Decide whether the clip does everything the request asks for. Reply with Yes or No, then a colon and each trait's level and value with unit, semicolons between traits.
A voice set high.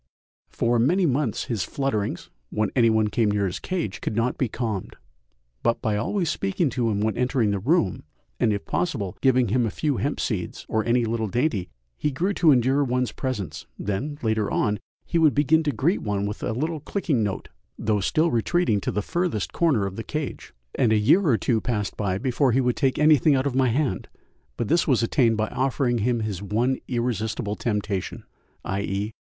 No: low, 120 Hz